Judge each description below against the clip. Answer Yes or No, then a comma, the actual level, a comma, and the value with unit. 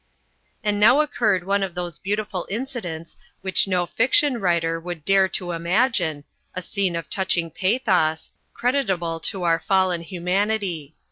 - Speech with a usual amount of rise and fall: Yes, average, 3.3 semitones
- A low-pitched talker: No, medium, 185 Hz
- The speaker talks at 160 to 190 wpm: No, average, 140 wpm